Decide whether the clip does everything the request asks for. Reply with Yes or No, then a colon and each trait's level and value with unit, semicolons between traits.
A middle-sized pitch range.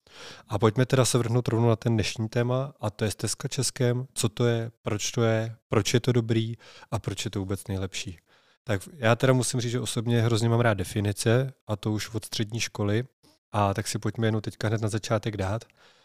No: narrow, 1.9 semitones